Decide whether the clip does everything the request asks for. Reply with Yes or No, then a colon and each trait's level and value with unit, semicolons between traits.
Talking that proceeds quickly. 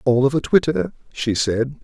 No: average, 195 wpm